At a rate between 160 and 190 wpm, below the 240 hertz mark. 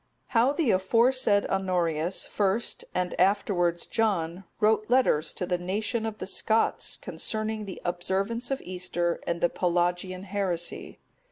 No: slow, 135 wpm; high, 190 Hz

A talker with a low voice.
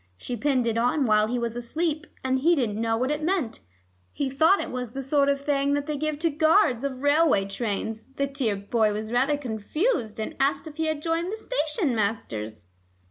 No: very high, 270 Hz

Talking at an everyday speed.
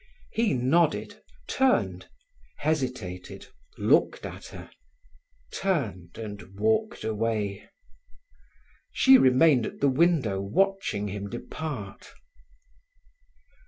No: slow, 85 wpm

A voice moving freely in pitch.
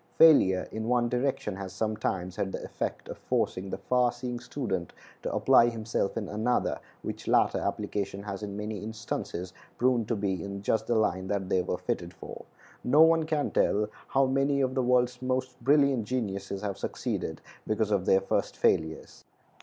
No: average, 4.4 semitones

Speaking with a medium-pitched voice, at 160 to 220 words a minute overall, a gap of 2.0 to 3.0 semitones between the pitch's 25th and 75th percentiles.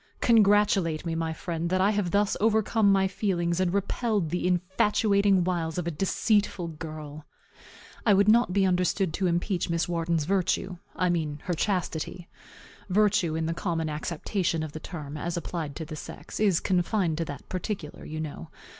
No: medium, 175 Hz; average, 170 wpm; average, 3.5 semitones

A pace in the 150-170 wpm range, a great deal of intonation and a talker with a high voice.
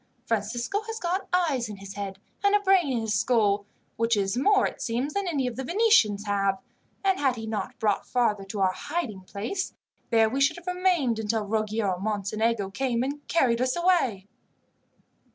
No: average, 185 wpm; wide, 8.1 semitones; high, 235 Hz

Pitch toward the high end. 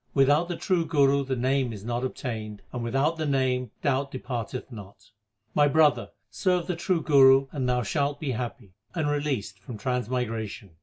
No: low, 130 Hz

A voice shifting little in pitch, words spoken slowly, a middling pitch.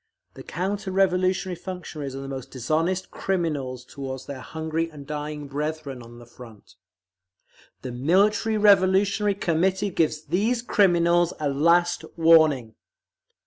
No: average, 5.1 semitones; slow, 125 wpm; medium, 165 Hz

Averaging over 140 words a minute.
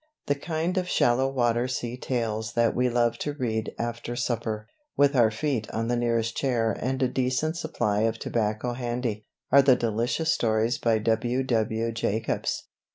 Yes: average, 160 wpm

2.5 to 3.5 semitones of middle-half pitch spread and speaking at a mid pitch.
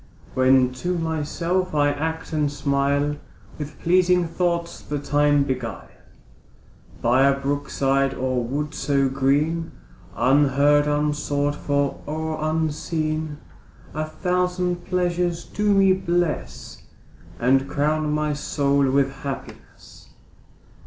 Yes: average, 2.9 semitones; medium, 150 Hz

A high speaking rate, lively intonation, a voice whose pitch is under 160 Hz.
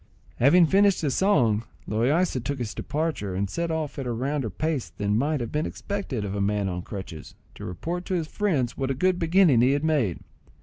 Yes: fast, 210 wpm; wide, 7.2 semitones; low, 135 Hz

